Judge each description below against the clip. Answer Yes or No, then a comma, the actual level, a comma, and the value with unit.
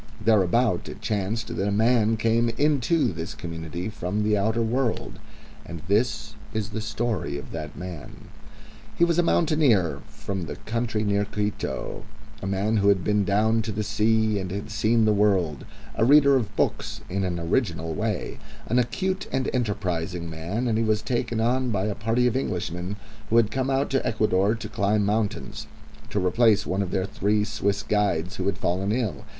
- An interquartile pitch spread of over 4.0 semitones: No, average, 3.1 semitones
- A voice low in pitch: Yes, low, 105 Hz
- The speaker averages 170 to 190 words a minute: Yes, average, 180 wpm